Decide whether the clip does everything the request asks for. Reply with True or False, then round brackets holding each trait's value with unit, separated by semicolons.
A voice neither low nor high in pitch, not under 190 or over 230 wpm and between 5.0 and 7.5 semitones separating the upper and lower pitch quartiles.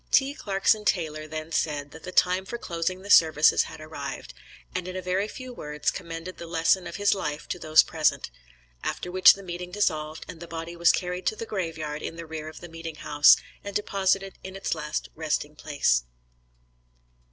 False (170 Hz; 195 wpm; 3.4 semitones)